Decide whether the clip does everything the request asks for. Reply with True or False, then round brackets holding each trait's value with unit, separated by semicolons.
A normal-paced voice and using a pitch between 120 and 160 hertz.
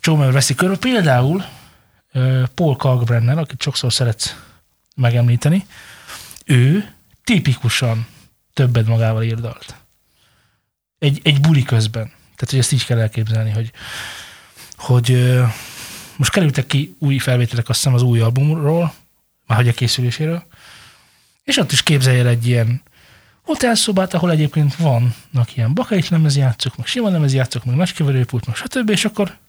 True (140 wpm; 130 Hz)